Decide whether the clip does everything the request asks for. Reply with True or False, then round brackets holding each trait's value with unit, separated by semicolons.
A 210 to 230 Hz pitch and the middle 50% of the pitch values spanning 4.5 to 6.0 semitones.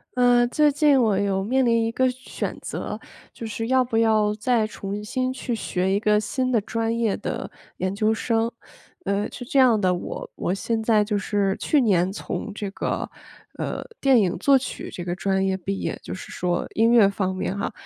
False (220 Hz; 3.6 semitones)